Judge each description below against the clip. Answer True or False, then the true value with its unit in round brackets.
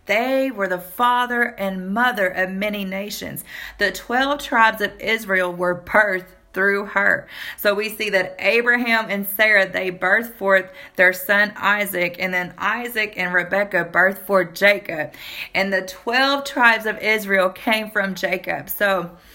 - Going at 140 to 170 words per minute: True (150 wpm)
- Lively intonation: False (2.7 semitones)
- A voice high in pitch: True (200 Hz)